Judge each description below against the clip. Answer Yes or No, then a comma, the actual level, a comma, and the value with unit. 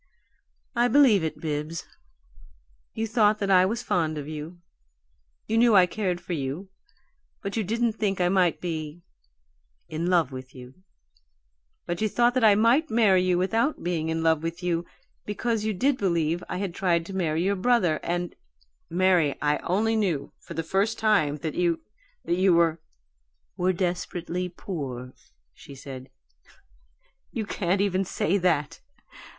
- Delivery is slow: No, average, 165 wpm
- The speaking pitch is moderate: Yes, medium, 180 Hz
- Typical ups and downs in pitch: Yes, average, 4.2 semitones